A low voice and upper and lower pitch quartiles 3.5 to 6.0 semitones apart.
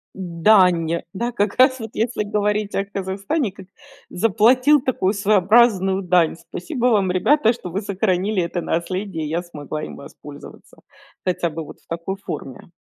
No: high, 195 Hz; average, 3.8 semitones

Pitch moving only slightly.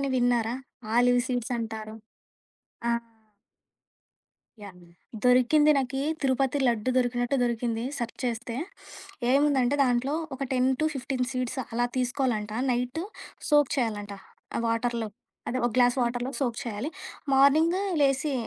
Yes: narrow, 2.2 semitones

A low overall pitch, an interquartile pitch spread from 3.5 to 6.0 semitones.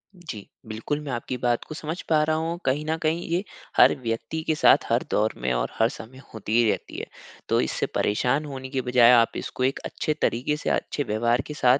Yes: low, 130 Hz; average, 4.8 semitones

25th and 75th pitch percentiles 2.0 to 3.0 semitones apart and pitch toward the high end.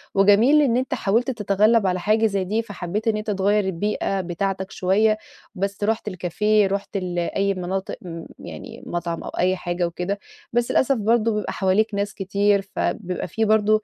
Yes: narrow, 2.5 semitones; high, 200 Hz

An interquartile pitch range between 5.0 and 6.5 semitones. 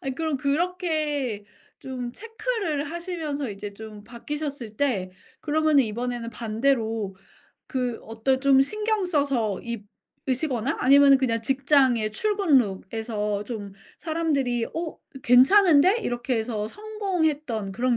Yes: wide, 5.4 semitones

